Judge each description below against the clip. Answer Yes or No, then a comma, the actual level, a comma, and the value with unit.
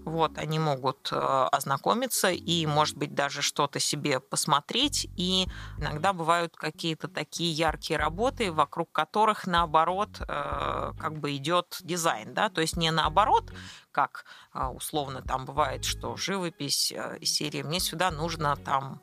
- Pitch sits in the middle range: Yes, medium, 160 Hz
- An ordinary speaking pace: Yes, average, 130 wpm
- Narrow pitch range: No, average, 3.5 semitones